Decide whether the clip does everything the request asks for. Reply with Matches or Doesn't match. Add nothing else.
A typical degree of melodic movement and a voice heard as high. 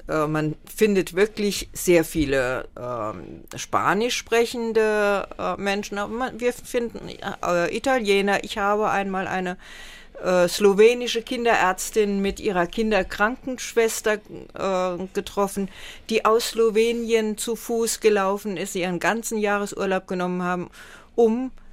Matches